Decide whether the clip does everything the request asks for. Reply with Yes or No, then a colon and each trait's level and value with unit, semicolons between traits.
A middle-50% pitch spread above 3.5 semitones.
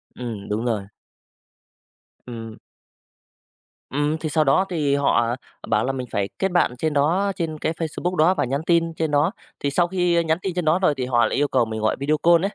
Yes: average, 5.1 semitones